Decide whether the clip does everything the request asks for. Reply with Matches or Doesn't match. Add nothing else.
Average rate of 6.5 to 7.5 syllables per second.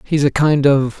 Doesn't match